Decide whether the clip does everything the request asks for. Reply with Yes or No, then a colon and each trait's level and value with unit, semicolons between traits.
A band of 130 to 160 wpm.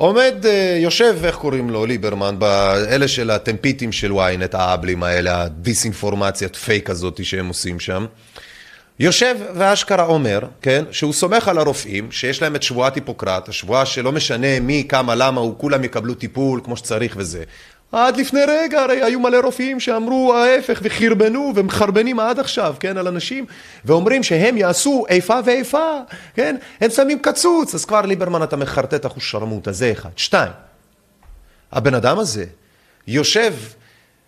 Yes: average, 145 wpm